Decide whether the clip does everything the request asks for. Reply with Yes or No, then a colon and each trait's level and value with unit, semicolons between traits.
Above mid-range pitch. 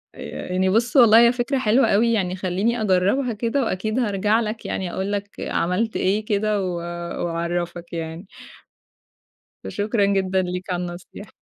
Yes: high, 200 Hz